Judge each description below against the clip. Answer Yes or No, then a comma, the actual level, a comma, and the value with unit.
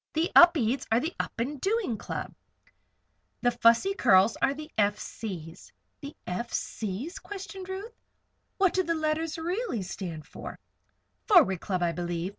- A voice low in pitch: No, very high, 270 Hz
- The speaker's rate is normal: Yes, average, 150 wpm